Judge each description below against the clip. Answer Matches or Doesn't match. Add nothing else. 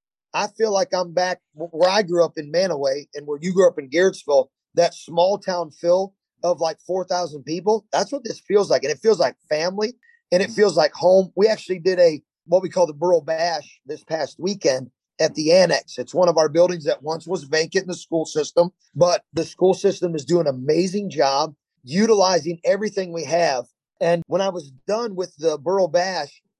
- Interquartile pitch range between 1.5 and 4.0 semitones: Matches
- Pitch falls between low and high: Matches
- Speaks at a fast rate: Matches